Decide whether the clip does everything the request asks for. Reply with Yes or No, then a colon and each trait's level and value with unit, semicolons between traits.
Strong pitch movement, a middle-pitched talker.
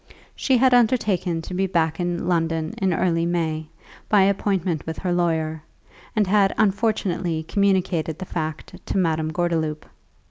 No: average, 3.2 semitones; medium, 175 Hz